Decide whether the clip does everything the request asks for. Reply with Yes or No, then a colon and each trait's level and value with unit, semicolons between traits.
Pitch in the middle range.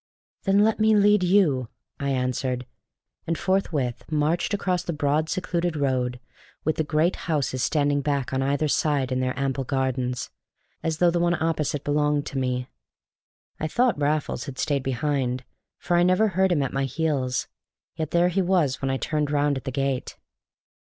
Yes: medium, 145 Hz